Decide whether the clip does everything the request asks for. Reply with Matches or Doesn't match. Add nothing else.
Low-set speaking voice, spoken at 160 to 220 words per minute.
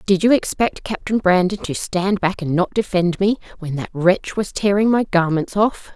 Doesn't match